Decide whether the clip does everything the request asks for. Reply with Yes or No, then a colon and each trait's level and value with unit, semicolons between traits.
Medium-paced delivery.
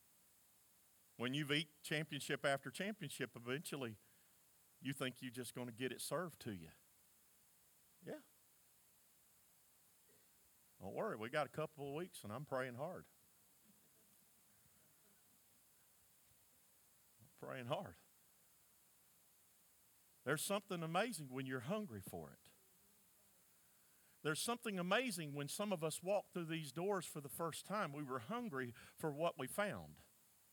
No: slow, 125 wpm